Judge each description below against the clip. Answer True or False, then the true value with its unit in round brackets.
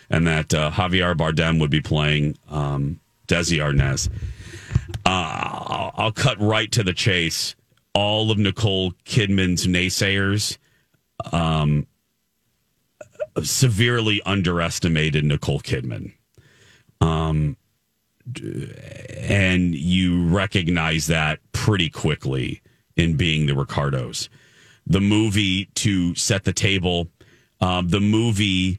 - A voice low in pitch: True (90 Hz)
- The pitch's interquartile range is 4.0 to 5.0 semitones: True (4.7 semitones)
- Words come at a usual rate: False (100 wpm)